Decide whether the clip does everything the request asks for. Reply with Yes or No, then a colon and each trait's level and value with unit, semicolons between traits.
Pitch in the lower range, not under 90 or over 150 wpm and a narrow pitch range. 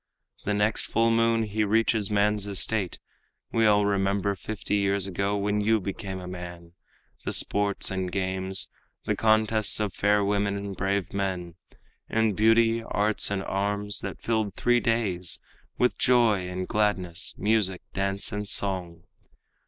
Yes: low, 100 Hz; average, 145 wpm; narrow, 2.1 semitones